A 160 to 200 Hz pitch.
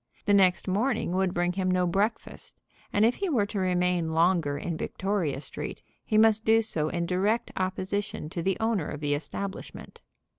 Yes: medium, 185 Hz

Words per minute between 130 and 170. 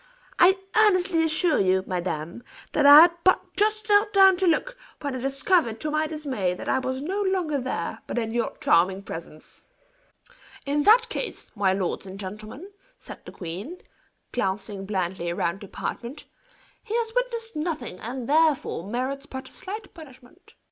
Yes: average, 160 wpm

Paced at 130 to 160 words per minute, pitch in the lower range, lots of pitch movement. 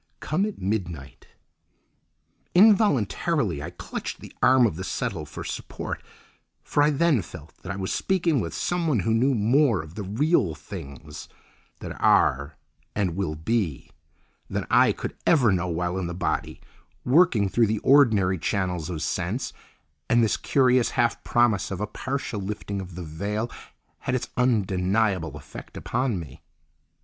Yes: average, 150 wpm; low, 100 Hz; wide, 6.4 semitones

